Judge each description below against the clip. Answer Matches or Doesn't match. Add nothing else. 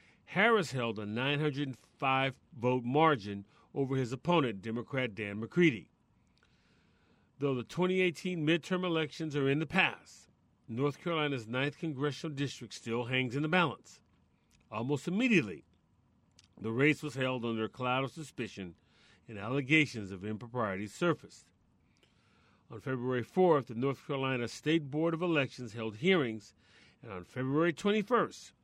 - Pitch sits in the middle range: Doesn't match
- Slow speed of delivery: Matches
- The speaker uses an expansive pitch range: Matches